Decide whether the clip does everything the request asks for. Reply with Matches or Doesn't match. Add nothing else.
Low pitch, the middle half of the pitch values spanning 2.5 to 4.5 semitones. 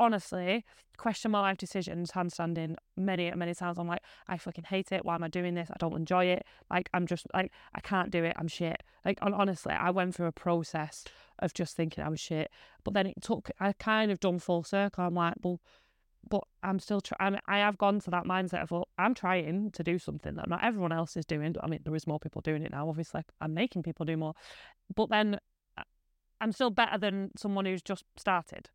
Doesn't match